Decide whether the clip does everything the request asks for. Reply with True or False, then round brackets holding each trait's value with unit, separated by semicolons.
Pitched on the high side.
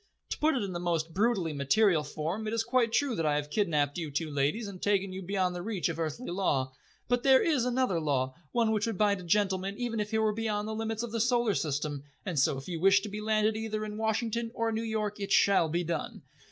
True (205 Hz)